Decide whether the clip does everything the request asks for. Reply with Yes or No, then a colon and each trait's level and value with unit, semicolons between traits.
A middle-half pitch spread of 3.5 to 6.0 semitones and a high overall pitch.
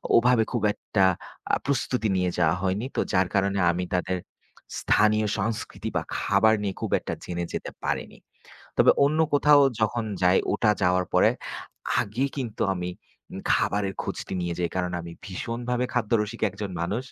No: average, 4.2 semitones; low, 105 Hz